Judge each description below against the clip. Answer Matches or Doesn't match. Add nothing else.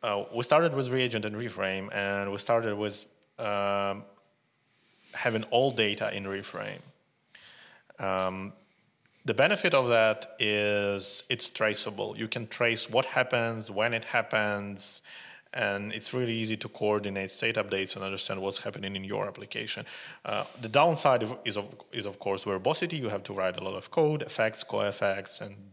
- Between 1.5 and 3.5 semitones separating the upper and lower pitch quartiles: Matches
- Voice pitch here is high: Doesn't match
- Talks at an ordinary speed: Matches